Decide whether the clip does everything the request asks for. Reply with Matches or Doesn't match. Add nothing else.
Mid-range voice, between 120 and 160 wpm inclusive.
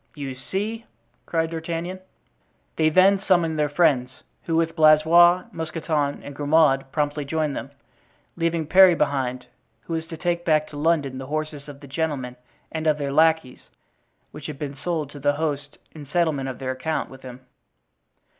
Doesn't match